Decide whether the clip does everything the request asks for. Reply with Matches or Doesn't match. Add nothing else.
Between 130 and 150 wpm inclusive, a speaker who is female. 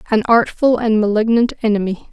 Matches